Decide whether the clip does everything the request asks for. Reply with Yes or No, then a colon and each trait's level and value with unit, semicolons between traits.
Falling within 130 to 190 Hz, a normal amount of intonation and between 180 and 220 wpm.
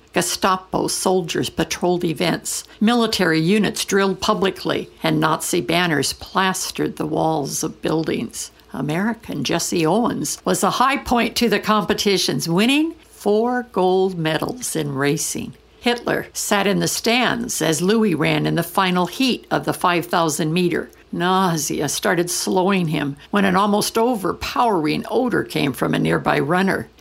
No: medium, 185 Hz; average, 4.1 semitones; average, 140 wpm